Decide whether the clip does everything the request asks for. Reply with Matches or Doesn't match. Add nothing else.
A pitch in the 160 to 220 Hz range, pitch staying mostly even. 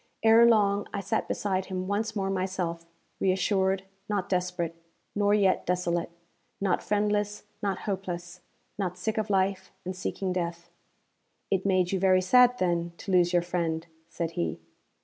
Matches